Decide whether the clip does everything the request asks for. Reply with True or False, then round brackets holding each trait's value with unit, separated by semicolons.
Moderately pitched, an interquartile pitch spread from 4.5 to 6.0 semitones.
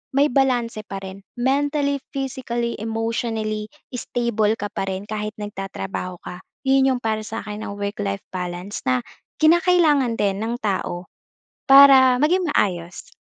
False (225 Hz; 4.8 semitones)